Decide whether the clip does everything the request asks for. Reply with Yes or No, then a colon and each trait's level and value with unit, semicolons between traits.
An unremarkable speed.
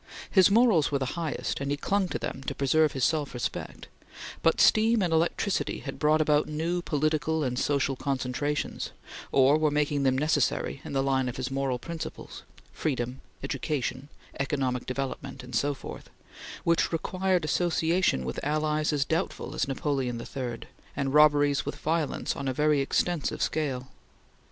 Yes: average, 160 wpm